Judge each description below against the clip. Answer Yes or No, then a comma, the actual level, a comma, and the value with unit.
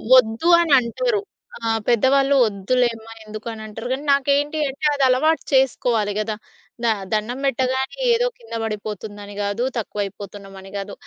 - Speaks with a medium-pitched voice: No, high, 230 Hz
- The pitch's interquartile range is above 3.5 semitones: Yes, average, 4.2 semitones